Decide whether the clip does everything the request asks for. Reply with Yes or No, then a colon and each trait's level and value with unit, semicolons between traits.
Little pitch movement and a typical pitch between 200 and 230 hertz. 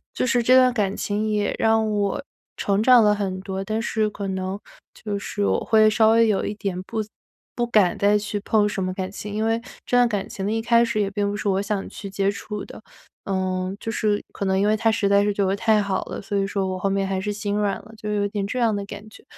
Yes: narrow, 1.7 semitones; high, 205 Hz